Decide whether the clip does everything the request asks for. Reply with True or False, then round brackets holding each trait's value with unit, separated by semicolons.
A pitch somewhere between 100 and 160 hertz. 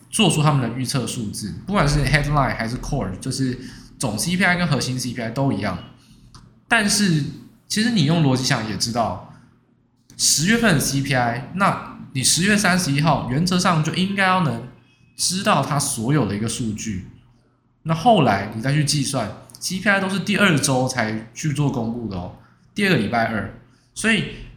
True (135 Hz)